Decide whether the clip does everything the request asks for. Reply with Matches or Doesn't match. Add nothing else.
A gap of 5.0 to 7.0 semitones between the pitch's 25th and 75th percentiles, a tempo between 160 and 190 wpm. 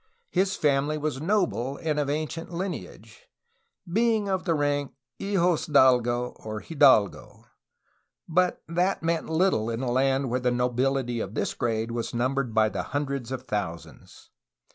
Doesn't match